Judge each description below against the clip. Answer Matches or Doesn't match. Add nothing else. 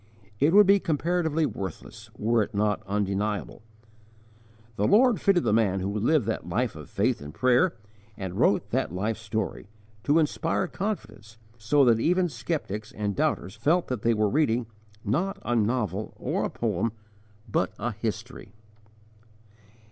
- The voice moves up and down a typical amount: Doesn't match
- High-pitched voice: Doesn't match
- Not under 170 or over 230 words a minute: Doesn't match